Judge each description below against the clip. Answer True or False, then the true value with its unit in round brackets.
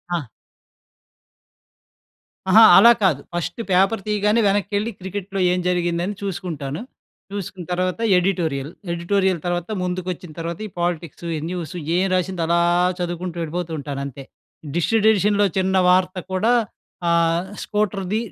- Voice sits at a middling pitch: True (180 Hz)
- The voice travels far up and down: False (2.5 semitones)